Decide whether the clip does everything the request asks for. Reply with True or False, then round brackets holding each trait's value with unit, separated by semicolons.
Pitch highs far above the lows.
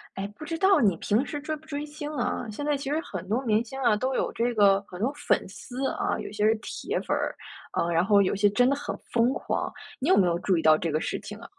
True (6.3 semitones)